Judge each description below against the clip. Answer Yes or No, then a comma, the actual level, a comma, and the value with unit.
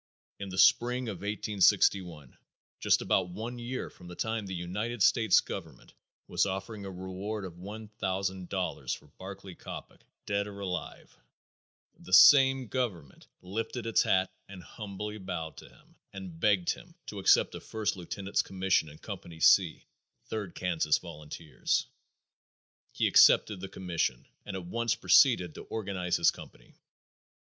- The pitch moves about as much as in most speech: Yes, average, 3.0 semitones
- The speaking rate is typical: Yes, average, 150 wpm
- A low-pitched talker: Yes, very low, 95 Hz